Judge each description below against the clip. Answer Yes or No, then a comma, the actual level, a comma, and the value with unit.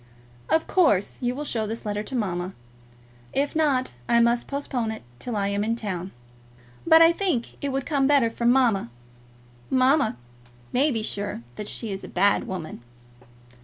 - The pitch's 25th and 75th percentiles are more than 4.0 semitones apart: Yes, average, 5.1 semitones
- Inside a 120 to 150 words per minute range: No, average, 170 wpm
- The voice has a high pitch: Yes, high, 235 Hz